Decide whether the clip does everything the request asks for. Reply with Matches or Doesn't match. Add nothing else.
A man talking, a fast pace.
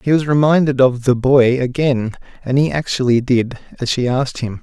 Doesn't match